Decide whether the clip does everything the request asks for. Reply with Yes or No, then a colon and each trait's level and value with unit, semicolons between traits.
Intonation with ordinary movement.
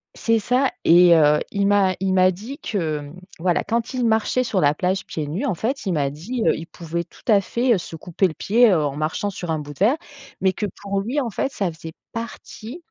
No: wide, 5.8 semitones